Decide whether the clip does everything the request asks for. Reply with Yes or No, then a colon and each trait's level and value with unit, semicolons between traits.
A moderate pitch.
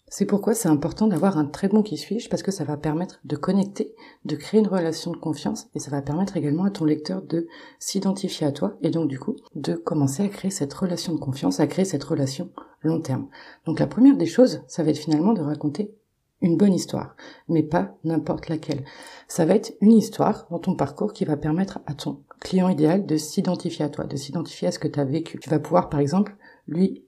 Yes: medium, 165 Hz